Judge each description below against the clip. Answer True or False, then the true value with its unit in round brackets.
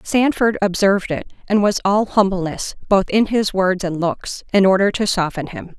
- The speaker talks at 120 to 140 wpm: False (185 wpm)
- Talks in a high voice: True (195 Hz)